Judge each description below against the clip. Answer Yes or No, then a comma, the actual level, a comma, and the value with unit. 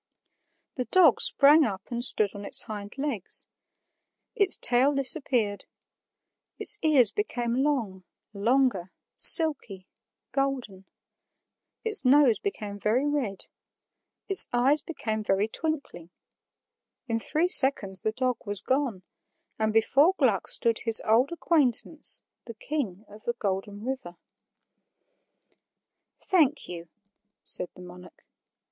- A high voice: Yes, high, 240 Hz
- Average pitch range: No, wide, 5.8 semitones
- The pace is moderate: No, slow, 115 wpm